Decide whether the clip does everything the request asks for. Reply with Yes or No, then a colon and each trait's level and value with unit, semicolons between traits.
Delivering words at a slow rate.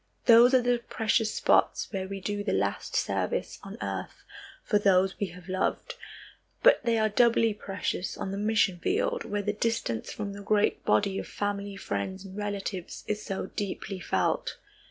No: average, 170 wpm